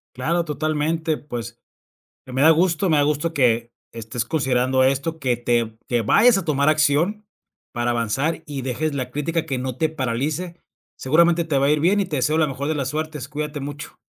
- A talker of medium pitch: Yes, medium, 145 Hz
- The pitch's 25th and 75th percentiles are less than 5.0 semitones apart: Yes, average, 3.8 semitones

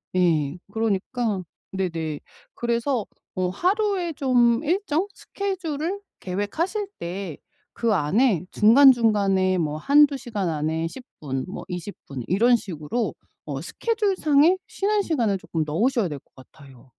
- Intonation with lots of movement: Yes, wide, 8.5 semitones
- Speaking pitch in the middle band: No, high, 220 Hz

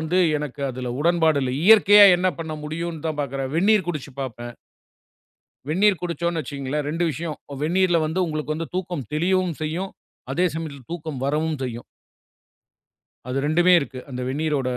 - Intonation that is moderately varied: Yes, average, 3.7 semitones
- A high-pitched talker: No, medium, 160 Hz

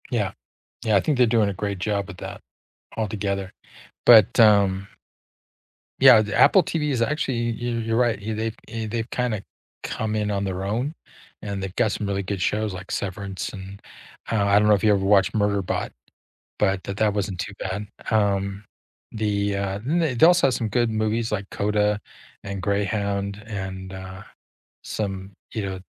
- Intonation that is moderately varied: No, narrow, 2.2 semitones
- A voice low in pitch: Yes, low, 105 Hz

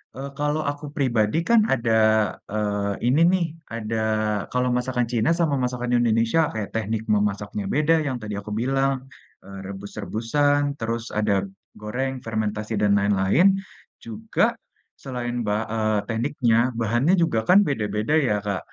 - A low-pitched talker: Yes, low, 115 Hz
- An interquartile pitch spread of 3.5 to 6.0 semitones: Yes, average, 4.2 semitones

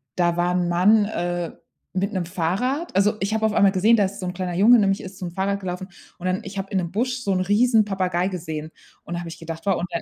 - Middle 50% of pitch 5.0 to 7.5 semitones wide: No, narrow, 2.6 semitones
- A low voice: No, high, 190 Hz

